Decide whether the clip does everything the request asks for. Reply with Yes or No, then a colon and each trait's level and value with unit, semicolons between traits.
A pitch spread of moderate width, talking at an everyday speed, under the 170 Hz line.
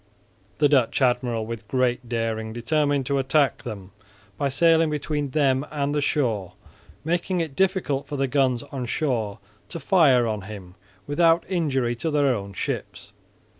Yes: average, 4.3 semitones; average, 155 wpm; low, 135 Hz